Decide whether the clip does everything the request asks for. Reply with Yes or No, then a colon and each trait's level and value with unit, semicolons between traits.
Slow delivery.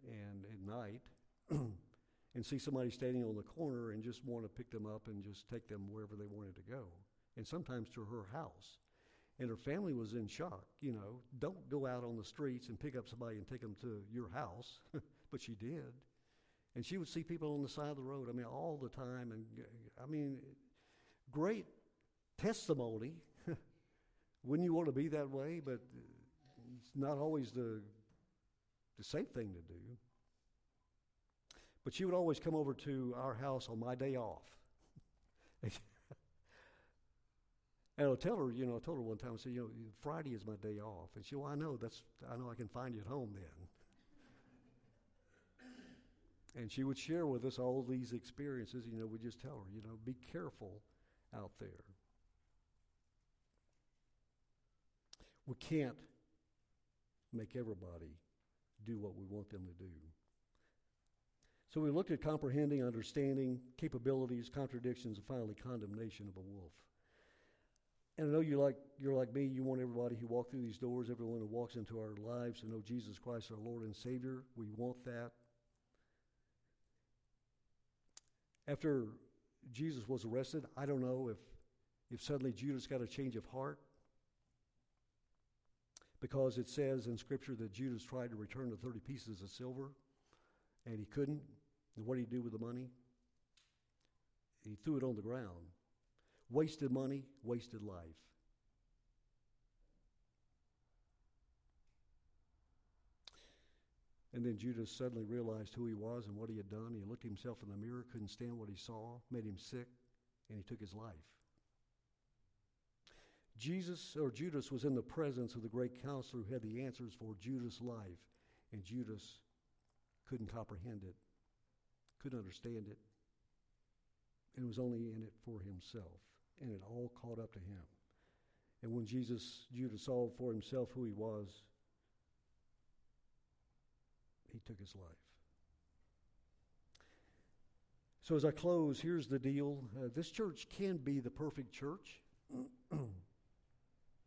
No: average, 155 wpm